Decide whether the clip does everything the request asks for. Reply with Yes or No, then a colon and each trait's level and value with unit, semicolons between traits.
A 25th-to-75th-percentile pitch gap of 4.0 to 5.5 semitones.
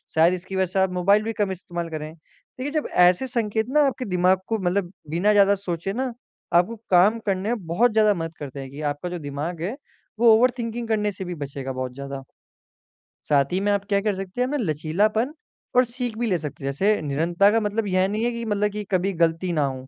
Yes: average, 4.7 semitones